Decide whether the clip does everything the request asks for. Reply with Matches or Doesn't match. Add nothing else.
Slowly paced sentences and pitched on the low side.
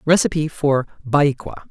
Doesn't match